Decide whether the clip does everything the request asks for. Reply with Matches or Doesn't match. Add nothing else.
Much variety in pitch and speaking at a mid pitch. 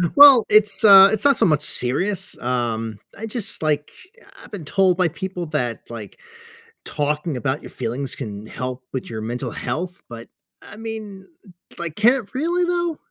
Matches